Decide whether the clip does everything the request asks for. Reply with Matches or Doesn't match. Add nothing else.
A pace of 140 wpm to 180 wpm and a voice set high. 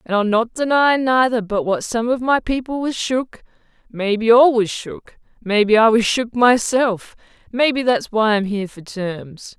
Matches